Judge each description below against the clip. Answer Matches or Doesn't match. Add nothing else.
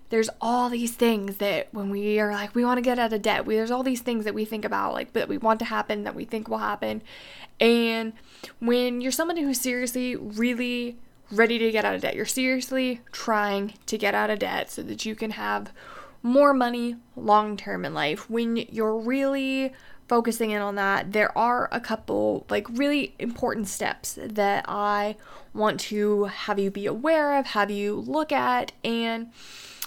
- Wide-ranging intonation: Doesn't match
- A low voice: Doesn't match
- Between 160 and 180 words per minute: Doesn't match